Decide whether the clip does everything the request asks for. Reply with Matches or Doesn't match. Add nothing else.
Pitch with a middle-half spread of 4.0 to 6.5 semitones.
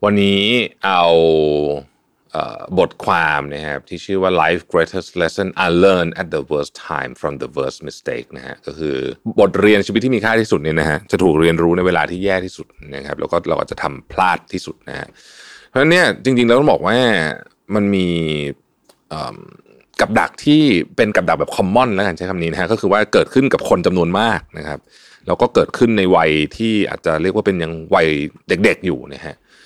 Matches